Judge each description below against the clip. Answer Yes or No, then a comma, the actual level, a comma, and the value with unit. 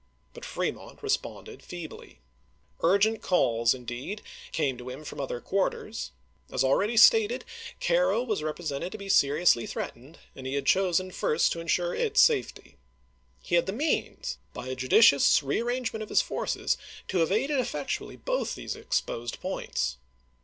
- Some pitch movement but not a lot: No, wide, 8.5 semitones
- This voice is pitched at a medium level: Yes, medium, 175 Hz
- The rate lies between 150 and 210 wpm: Yes, average, 160 wpm